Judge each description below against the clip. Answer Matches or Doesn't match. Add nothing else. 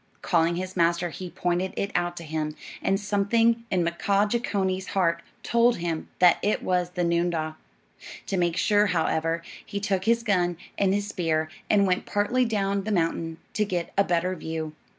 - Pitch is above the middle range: Doesn't match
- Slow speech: Doesn't match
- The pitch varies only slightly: Doesn't match